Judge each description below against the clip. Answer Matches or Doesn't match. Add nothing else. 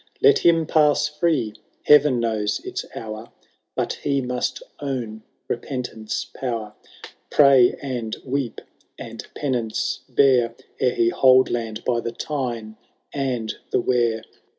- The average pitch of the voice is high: Doesn't match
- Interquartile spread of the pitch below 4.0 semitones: Matches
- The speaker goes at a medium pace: Doesn't match